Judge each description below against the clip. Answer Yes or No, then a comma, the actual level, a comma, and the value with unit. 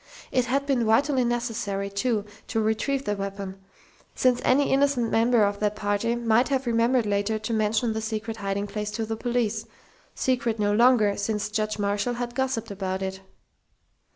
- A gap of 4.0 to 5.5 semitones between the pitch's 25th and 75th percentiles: No, average, 2.9 semitones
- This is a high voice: Yes, high, 225 Hz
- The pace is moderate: Yes, average, 170 wpm